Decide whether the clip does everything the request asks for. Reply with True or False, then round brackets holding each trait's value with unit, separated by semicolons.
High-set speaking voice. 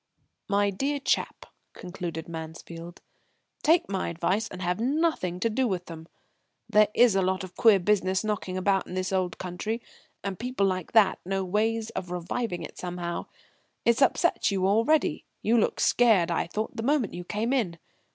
True (195 Hz)